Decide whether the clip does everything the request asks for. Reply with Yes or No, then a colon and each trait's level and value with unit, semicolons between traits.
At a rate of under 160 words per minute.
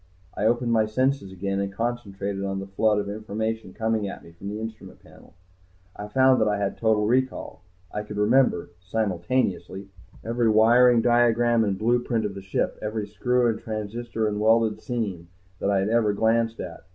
No: average, 180 wpm